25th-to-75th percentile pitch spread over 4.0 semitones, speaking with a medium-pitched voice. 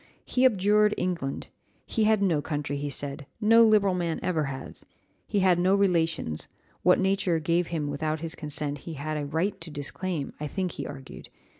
Yes: average, 4.7 semitones; medium, 165 Hz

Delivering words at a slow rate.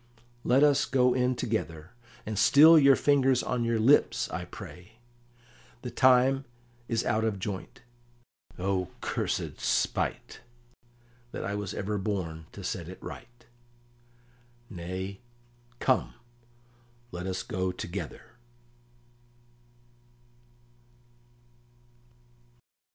Yes: slow, 100 wpm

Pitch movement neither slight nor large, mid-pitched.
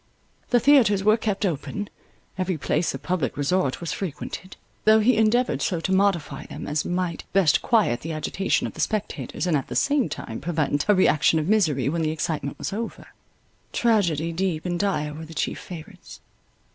Yes: average, 5.0 semitones; medium, 180 Hz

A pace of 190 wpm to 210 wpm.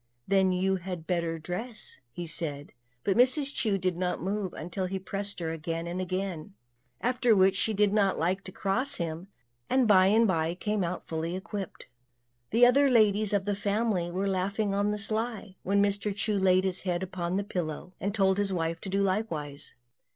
Yes: average, 195 wpm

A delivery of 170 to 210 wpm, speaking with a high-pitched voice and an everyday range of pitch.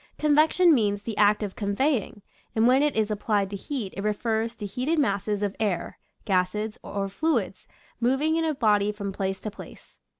Yes: average, 180 wpm; high, 215 Hz; average, 4.6 semitones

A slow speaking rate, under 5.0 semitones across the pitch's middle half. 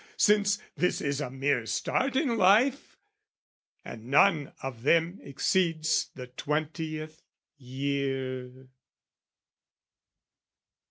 No: slow, 90 wpm; average, 5.3 semitones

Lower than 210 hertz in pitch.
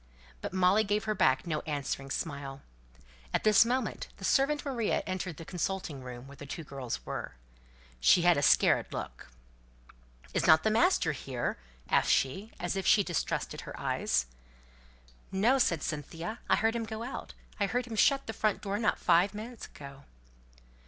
Yes: medium, 185 Hz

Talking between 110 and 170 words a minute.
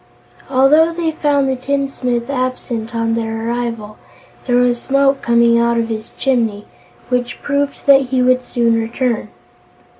Yes: average, 145 wpm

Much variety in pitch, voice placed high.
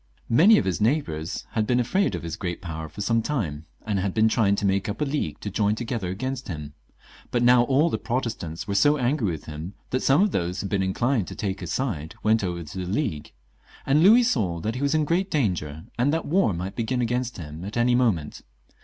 No: wide, 6.5 semitones; low, 110 Hz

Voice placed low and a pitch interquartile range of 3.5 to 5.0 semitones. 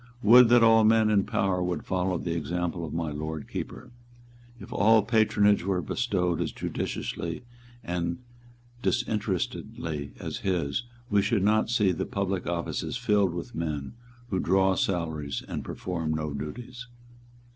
Yes: very low, 95 Hz; average, 4.4 semitones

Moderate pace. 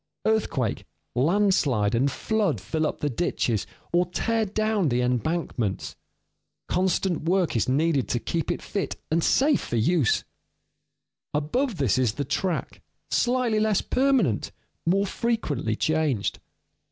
No: slow, 130 wpm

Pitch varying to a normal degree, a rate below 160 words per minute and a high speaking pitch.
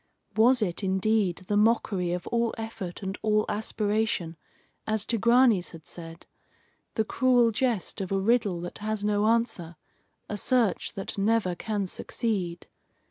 Yes: average, 3.3 semitones; average, 140 wpm; high, 210 Hz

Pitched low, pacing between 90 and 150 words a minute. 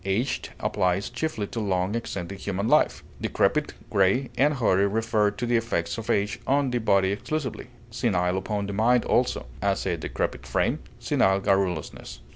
No: low, 100 Hz; average, 160 wpm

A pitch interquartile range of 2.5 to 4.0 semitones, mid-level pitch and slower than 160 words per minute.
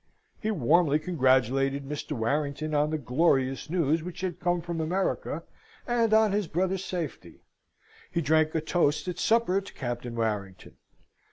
No: average, 4.9 semitones; medium, 155 Hz; average, 150 wpm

